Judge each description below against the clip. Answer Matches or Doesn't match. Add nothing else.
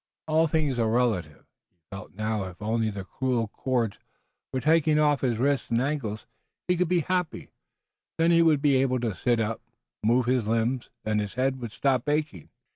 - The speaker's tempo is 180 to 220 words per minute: Matches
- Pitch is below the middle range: Matches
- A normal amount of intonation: Matches